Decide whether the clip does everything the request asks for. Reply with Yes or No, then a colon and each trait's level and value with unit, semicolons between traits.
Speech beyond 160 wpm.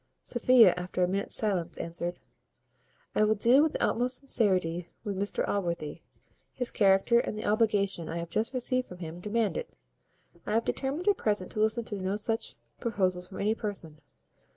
Yes: average, 175 wpm